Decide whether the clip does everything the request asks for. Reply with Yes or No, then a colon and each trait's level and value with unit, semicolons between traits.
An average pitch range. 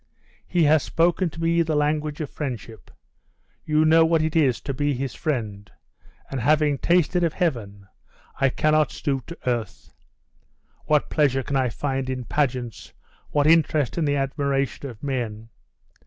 Yes: average, 3.5 semitones